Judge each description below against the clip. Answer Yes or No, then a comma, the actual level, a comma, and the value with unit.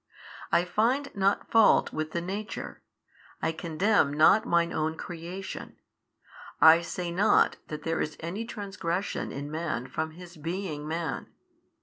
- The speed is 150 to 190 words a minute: No, average, 140 wpm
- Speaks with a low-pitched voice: No, medium, 170 Hz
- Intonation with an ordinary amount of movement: Yes, average, 3.6 semitones